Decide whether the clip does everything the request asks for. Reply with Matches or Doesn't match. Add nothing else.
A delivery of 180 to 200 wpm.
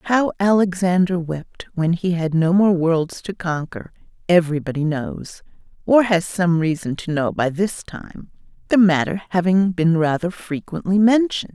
Doesn't match